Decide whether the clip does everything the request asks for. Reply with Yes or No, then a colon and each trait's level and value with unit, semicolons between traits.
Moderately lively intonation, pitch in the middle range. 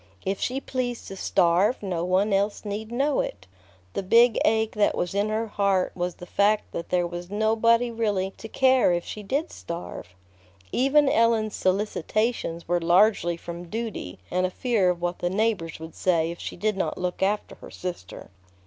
No: average, 4.1 semitones; high, 200 Hz